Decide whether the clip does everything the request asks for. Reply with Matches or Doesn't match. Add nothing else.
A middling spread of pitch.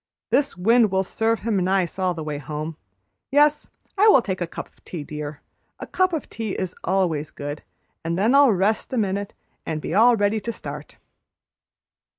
Doesn't match